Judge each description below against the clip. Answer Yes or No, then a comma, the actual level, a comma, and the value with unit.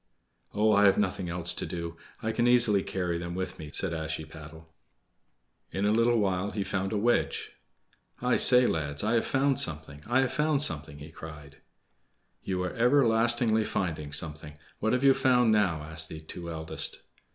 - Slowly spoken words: No, average, 175 wpm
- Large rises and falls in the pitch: Yes, wide, 6.4 semitones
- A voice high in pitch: No, very low, 95 Hz